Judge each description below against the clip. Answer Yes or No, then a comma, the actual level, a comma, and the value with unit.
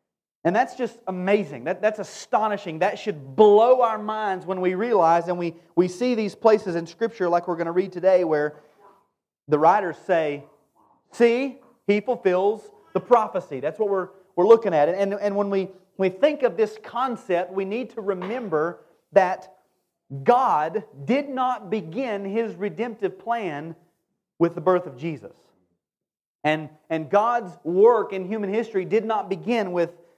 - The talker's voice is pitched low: No, high, 195 Hz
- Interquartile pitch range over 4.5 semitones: No, average, 4.2 semitones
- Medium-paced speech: Yes, average, 165 wpm